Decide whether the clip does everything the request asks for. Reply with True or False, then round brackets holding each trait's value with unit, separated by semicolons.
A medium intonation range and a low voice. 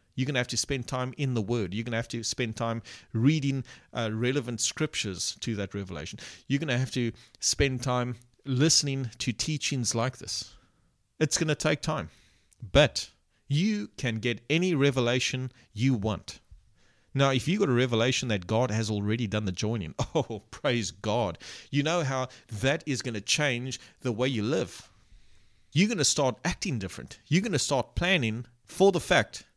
True (3.9 semitones; 120 Hz)